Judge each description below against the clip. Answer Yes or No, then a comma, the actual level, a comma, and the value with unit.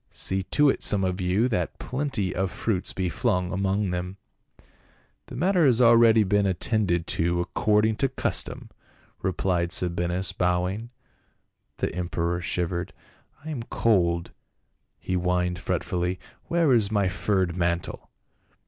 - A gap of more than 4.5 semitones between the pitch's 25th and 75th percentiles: No, average, 3.8 semitones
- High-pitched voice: No, very low, 95 Hz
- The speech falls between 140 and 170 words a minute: Yes, average, 145 wpm